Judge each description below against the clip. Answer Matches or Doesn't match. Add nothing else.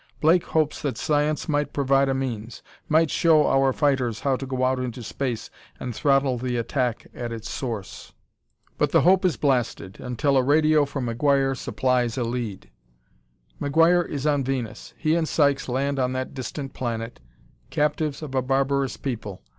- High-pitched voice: Doesn't match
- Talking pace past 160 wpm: Matches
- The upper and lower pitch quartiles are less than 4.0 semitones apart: Matches